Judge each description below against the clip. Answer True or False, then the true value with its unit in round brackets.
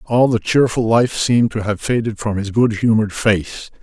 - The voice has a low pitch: True (110 Hz)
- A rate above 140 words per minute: True (205 wpm)